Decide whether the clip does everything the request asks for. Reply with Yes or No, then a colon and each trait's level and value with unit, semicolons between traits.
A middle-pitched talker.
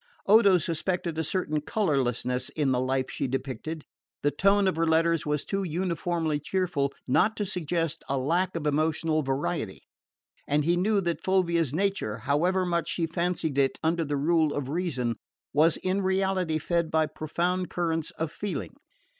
Yes: medium, 165 Hz